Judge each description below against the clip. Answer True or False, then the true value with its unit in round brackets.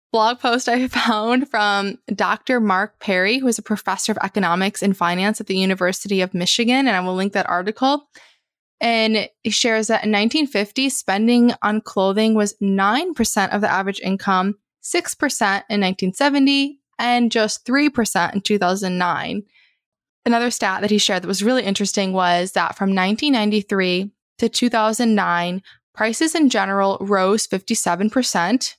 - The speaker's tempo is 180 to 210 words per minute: False (145 wpm)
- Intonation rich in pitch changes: False (3.6 semitones)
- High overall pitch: True (210 Hz)